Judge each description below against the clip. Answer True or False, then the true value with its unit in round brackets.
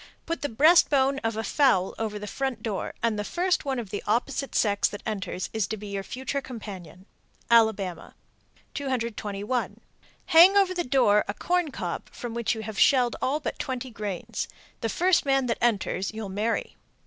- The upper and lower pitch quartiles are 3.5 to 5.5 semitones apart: True (4.6 semitones)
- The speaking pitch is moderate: False (230 Hz)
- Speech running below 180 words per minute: False (185 wpm)